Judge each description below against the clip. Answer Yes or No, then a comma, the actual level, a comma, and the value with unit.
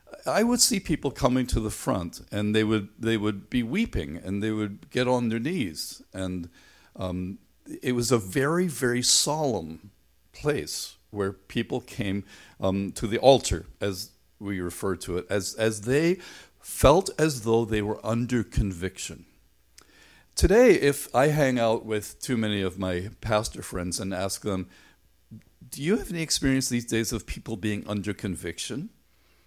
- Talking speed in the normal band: Yes, average, 165 wpm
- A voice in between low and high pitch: No, low, 110 Hz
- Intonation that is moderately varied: Yes, average, 4.8 semitones